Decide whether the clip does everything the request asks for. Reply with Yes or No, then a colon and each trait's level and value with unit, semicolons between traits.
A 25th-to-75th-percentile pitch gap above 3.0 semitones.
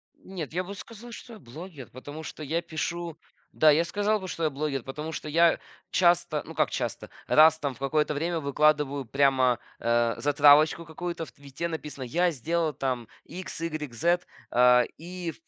Yes: average, 3.6 semitones